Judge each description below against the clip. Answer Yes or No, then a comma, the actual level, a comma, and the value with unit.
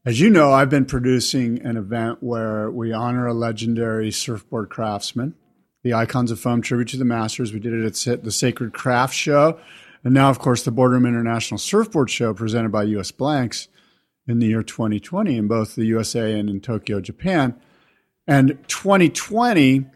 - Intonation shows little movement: No, average, 3.2 semitones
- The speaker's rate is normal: Yes, average, 175 wpm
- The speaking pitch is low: Yes, low, 120 Hz